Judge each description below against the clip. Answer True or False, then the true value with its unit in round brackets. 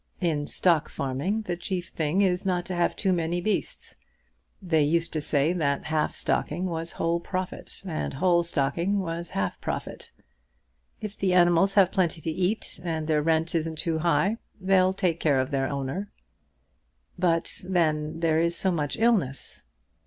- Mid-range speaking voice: True (170 Hz)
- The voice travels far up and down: False (2.9 semitones)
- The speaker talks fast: False (165 wpm)